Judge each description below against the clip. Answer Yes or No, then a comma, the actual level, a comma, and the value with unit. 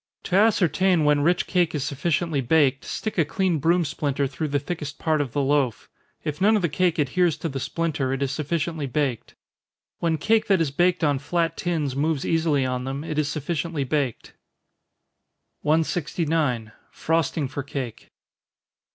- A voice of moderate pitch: Yes, medium, 150 Hz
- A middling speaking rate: Yes, average, 170 wpm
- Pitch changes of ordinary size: Yes, average, 3.3 semitones